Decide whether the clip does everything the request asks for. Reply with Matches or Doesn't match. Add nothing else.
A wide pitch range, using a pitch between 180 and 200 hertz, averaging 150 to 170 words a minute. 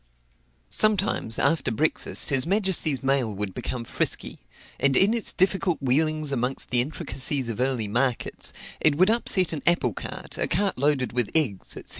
Doesn't match